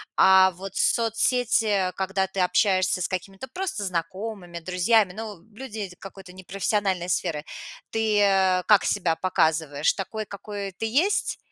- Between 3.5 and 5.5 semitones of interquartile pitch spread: No, average, 2.7 semitones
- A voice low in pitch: No, high, 195 Hz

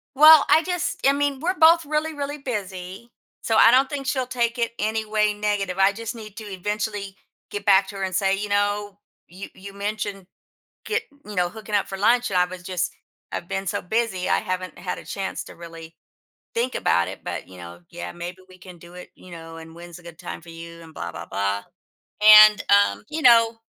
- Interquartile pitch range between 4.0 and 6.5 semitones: Yes, average, 4.3 semitones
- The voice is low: No, high, 200 Hz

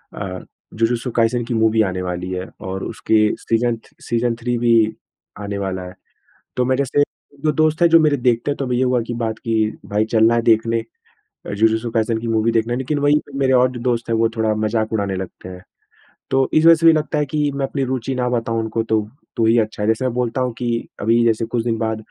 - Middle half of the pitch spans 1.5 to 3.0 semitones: Yes, narrow, 2.4 semitones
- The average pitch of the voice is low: Yes, low, 115 Hz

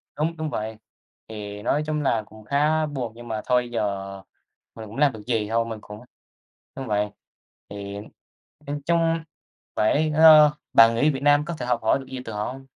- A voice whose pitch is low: Yes, low, 120 Hz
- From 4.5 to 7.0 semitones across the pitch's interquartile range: Yes, wide, 5.6 semitones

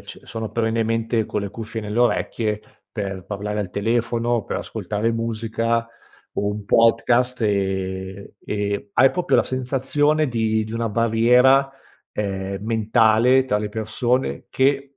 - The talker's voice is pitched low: Yes, low, 115 Hz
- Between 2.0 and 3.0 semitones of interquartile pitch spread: Yes, narrow, 2.5 semitones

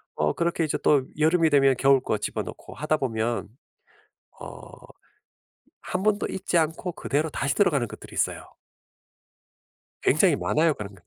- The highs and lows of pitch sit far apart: No, average, 3.9 semitones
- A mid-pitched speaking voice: Yes, medium, 150 Hz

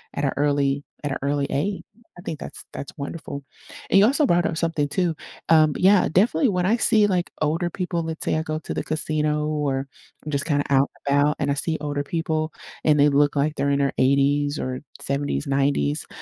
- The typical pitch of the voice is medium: Yes, medium, 150 Hz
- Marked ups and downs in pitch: No, average, 2.8 semitones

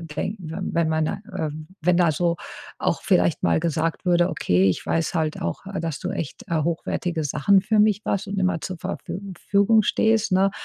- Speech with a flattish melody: No, average, 3.6 semitones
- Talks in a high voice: No, medium, 170 Hz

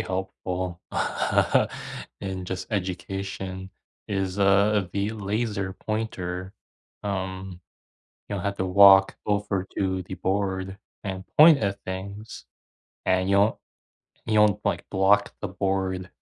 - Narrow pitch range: Yes, narrow, 1.3 semitones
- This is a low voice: Yes, very low, 95 Hz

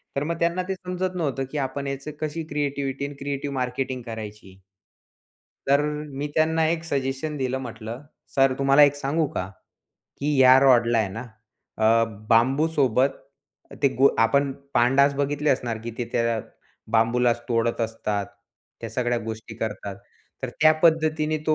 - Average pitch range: Yes, average, 4.0 semitones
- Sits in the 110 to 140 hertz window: Yes, low, 135 Hz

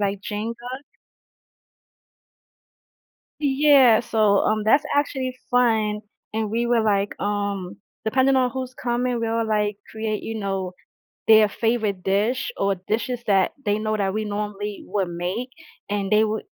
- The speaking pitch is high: Yes, high, 215 Hz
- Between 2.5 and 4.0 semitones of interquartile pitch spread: Yes, average, 2.9 semitones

